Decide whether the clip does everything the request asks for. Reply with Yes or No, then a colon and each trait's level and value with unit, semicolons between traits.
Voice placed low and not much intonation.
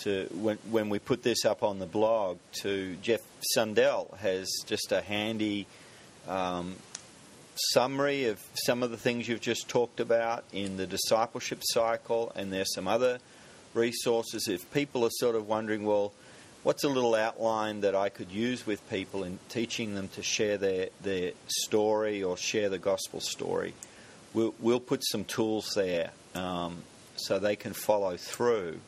No: low, 110 Hz; average, 3.0 semitones